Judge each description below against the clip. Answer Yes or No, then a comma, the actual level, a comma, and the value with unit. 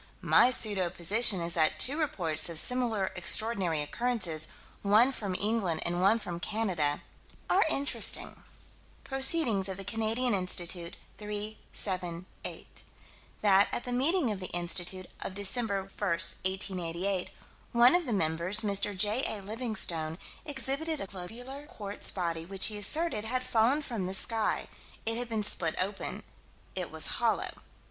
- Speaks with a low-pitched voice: No, high, 205 Hz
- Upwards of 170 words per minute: No, average, 140 wpm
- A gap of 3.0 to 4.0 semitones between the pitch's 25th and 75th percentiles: No, average, 4.7 semitones